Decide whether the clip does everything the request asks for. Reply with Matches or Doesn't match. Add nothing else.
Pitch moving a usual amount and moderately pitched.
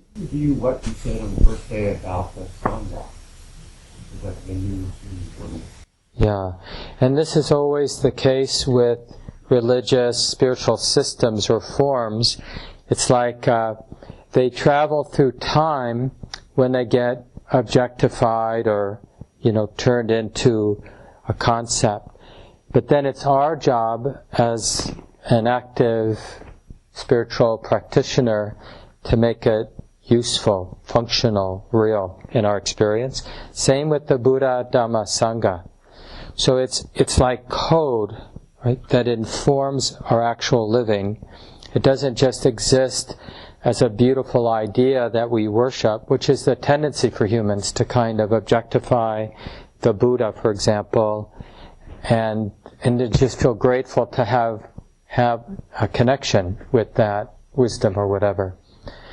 Doesn't match